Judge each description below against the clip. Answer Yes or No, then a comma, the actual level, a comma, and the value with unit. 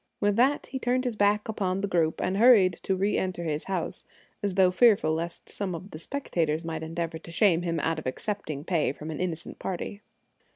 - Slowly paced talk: No, fast, 205 wpm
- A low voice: No, medium, 185 Hz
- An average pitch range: Yes, average, 3.9 semitones